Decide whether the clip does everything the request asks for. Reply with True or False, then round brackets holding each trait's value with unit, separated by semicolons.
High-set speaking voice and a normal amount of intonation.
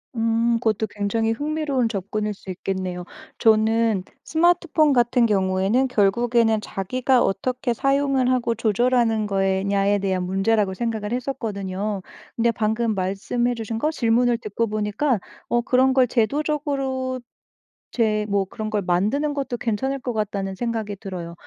True (225 Hz; 3.8 semitones)